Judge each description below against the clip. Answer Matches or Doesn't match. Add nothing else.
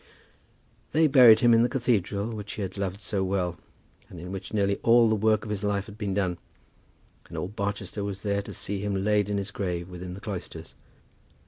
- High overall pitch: Doesn't match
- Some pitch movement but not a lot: Doesn't match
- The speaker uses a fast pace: Matches